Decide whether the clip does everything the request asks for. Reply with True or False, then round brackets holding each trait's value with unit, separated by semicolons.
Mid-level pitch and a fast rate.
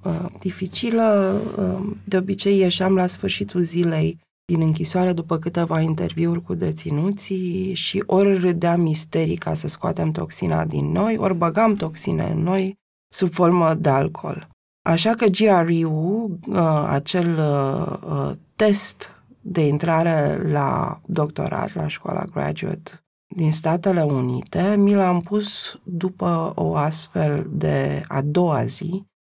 False (175 Hz; 120 wpm)